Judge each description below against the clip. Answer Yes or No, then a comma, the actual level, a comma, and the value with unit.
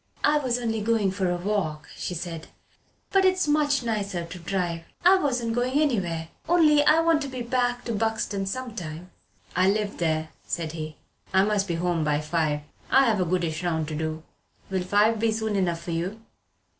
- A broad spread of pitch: Yes, wide, 6.4 semitones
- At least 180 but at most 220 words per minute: Yes, average, 190 wpm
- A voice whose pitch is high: Yes, high, 195 Hz